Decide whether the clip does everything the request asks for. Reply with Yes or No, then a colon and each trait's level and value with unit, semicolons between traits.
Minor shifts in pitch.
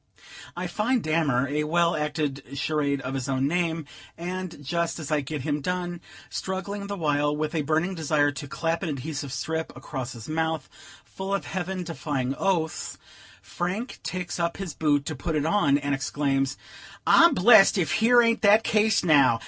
No: average, 3.9 semitones